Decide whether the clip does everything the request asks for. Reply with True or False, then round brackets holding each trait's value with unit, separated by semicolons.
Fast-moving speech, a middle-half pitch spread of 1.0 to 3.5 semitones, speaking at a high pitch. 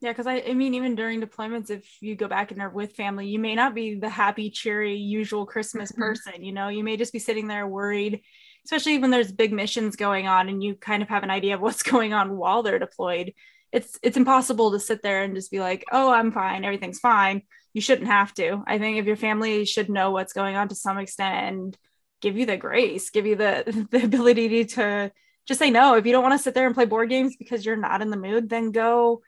True (250 wpm; 2.9 semitones; 215 Hz)